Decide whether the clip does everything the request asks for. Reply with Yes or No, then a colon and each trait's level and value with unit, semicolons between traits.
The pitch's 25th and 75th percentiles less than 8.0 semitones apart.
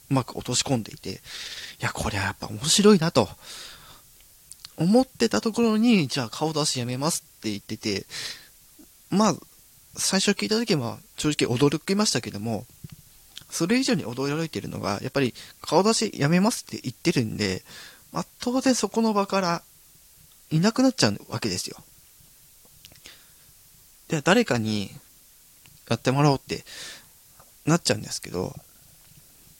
No: wide, 8.8 semitones